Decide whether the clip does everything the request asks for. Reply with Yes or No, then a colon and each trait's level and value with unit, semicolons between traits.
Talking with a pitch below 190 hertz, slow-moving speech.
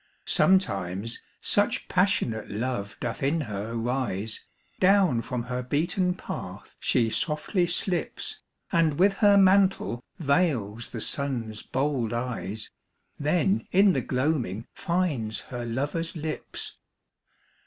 Yes: medium, 140 Hz; slow, 110 wpm